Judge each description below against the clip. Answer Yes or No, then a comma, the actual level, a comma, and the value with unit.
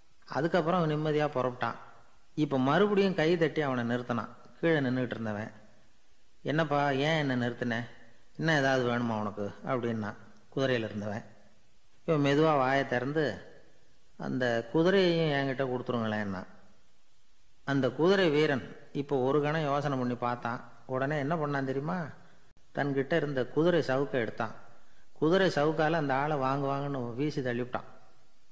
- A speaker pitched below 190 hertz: Yes, low, 135 Hz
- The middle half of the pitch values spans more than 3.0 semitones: Yes, average, 4.2 semitones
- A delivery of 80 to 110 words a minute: No, average, 120 wpm